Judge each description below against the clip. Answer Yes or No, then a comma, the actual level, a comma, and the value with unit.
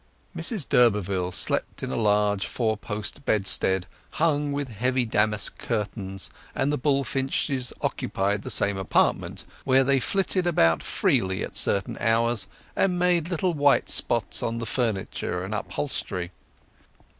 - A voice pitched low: Yes, low, 115 Hz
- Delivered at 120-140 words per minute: Yes, slow, 135 wpm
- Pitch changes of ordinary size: No, wide, 5.8 semitones